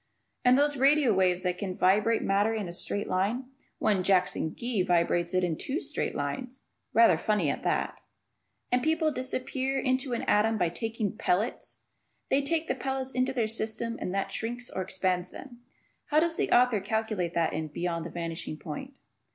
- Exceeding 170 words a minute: Yes, average, 180 wpm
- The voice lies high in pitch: Yes, high, 220 Hz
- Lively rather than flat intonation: Yes, wide, 6.0 semitones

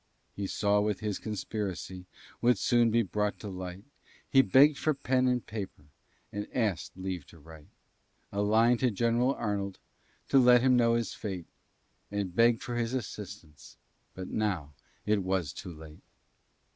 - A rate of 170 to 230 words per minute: No, average, 160 wpm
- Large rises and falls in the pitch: No, average, 4.2 semitones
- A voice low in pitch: Yes, low, 105 Hz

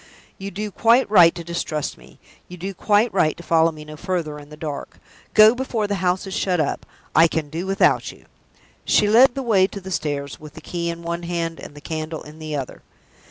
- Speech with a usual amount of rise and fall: Yes, average, 4.1 semitones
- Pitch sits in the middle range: Yes, medium, 170 Hz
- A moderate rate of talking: No, fast, 225 wpm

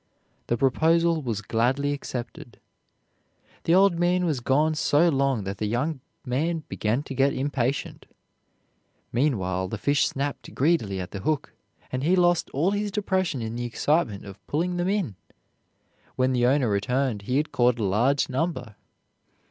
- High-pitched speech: No, low, 135 Hz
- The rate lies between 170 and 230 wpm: No, average, 155 wpm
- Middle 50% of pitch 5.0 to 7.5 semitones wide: Yes, wide, 5.4 semitones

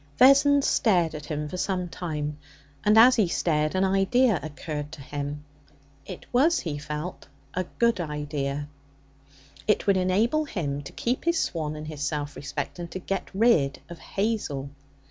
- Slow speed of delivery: No, average, 165 wpm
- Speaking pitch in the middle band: Yes, medium, 170 Hz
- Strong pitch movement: Yes, wide, 6.1 semitones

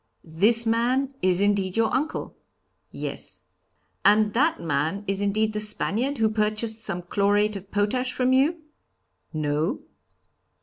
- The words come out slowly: Yes, slow, 130 wpm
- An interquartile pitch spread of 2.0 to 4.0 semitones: Yes, average, 3.1 semitones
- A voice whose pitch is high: Yes, high, 210 Hz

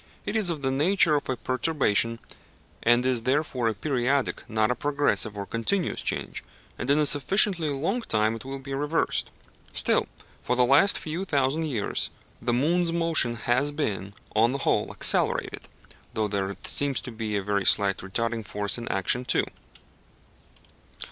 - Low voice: Yes, low, 130 Hz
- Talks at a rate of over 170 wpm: No, average, 165 wpm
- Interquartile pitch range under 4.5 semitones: No, average, 4.9 semitones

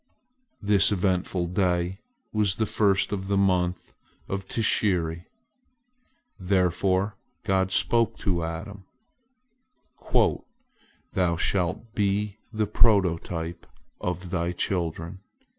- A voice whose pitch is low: Yes, very low, 95 Hz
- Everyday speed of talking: No, slow, 90 wpm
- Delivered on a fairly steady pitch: Yes, narrow, 2.3 semitones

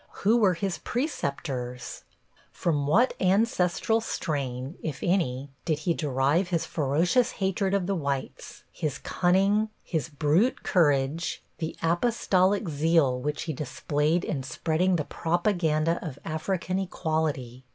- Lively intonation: No, average, 4.6 semitones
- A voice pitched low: No, medium, 165 Hz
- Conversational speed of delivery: No, slow, 125 wpm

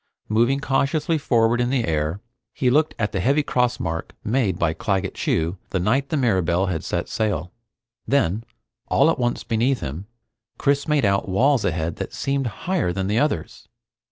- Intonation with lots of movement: Yes, wide, 6.8 semitones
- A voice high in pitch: No, low, 115 Hz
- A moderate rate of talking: Yes, average, 175 wpm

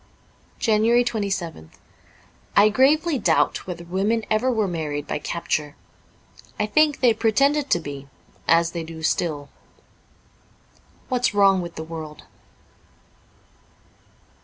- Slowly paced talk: Yes, slow, 125 wpm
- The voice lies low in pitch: No, high, 195 Hz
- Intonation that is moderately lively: No, wide, 6.3 semitones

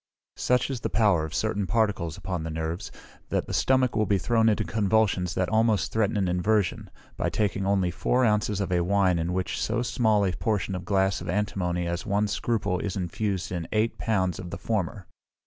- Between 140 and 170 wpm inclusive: No, average, 200 wpm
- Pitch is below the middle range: Yes, low, 100 Hz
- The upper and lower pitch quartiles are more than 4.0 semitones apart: No, average, 3.4 semitones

